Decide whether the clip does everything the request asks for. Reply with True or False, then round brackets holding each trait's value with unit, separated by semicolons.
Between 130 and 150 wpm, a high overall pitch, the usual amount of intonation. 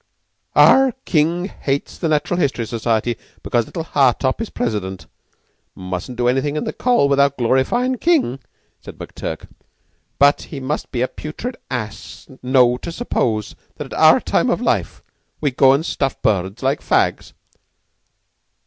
False (145 wpm; 135 Hz; 4.5 semitones)